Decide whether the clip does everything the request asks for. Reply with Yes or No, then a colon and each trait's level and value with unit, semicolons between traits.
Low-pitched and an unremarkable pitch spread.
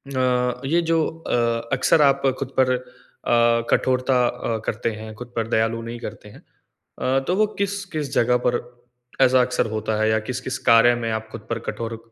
No: low, 125 Hz; narrow, 2.3 semitones